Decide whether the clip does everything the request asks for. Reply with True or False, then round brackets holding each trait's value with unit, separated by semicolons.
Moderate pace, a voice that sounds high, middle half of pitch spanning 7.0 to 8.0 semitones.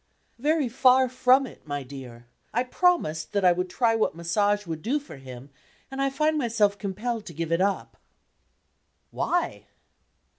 True (160 wpm; 205 Hz; 7.5 semitones)